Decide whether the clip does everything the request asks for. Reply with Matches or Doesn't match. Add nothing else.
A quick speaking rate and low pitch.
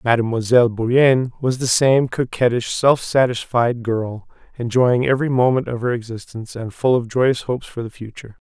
Doesn't match